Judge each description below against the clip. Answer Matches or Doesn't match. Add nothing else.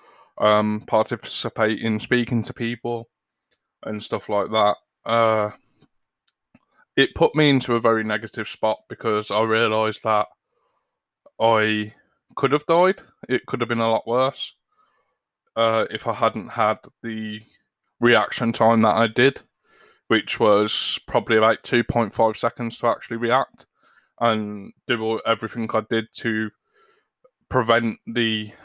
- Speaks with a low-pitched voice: Matches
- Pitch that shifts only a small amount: Matches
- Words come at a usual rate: Doesn't match